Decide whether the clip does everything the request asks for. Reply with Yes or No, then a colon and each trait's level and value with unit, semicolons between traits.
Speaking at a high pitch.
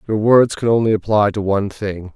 No: low, 105 Hz